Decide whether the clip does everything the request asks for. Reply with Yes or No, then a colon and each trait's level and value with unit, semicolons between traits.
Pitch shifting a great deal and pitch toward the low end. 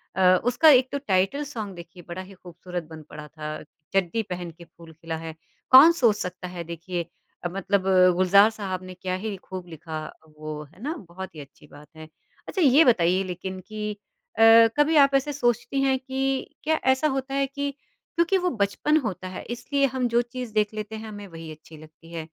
No: wide, 7.3 semitones; high, 195 Hz